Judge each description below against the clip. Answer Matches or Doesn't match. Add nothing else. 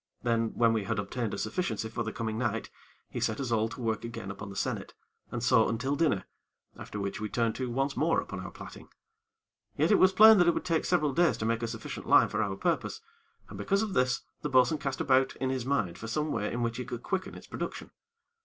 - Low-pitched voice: Matches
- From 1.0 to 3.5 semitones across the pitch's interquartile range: Doesn't match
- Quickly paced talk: Matches